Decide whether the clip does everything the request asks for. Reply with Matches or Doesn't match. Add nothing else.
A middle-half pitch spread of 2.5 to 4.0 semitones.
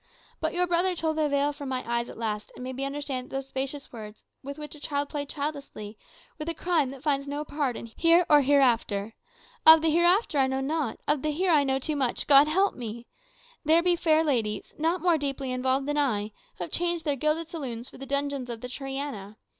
Matches